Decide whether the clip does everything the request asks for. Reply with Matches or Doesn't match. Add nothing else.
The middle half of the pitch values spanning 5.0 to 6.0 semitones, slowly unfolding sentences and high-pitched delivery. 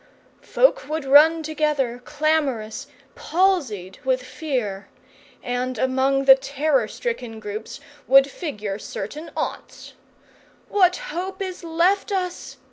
Matches